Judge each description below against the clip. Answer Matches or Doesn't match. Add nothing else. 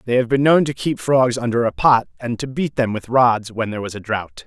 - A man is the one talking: Matches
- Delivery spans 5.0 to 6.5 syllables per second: Matches